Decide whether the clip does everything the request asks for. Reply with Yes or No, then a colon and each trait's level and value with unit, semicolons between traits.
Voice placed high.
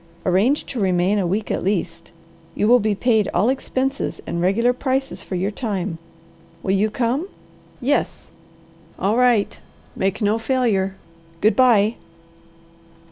Yes: high, 210 Hz